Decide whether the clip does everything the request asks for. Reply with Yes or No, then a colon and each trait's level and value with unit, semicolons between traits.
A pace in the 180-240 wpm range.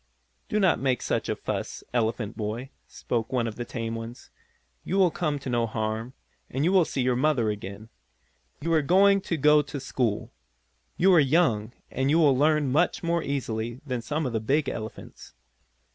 Yes: average, 190 wpm